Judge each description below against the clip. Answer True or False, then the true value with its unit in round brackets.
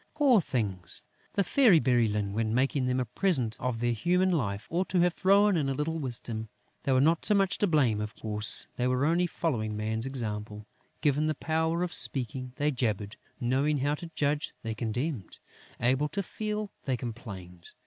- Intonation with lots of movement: True (6.6 semitones)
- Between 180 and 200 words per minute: True (185 wpm)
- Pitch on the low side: True (130 Hz)